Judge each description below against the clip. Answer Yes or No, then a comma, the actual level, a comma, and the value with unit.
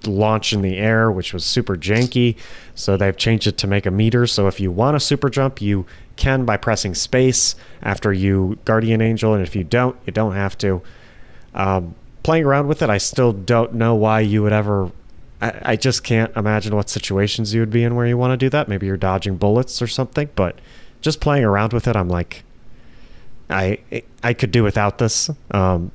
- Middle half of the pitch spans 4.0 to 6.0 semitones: No, average, 3.6 semitones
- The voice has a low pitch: Yes, low, 110 Hz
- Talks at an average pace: No, fast, 210 wpm